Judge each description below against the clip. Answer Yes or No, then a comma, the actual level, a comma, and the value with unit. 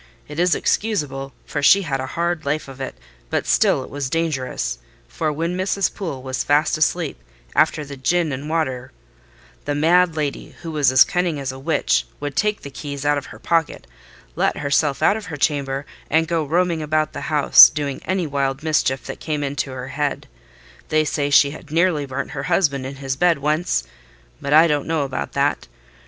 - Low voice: No, medium, 145 Hz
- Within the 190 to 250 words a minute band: Yes, average, 195 wpm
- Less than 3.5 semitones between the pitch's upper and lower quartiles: Yes, average, 3.0 semitones